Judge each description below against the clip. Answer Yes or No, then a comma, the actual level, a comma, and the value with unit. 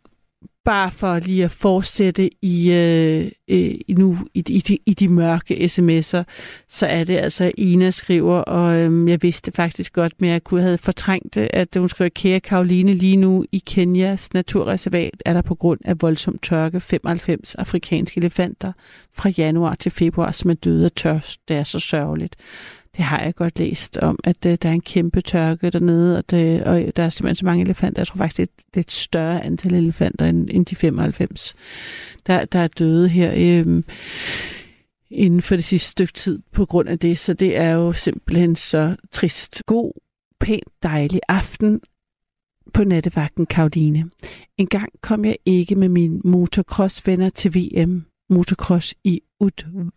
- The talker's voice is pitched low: No, medium, 175 Hz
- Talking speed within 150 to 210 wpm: Yes, average, 170 wpm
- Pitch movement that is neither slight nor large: No, narrow, 1.9 semitones